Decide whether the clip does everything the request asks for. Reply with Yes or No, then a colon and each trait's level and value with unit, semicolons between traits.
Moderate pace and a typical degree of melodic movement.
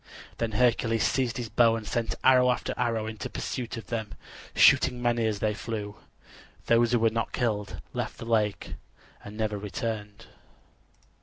No: average, 160 wpm; narrow, 1.8 semitones